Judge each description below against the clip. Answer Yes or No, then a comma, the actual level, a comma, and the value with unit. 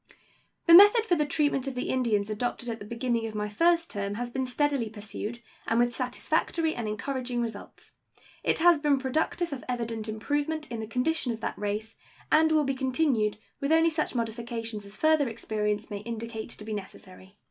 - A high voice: Yes, high, 240 Hz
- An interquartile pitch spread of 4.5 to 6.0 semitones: Yes, average, 5.1 semitones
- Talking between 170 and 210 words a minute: Yes, average, 190 wpm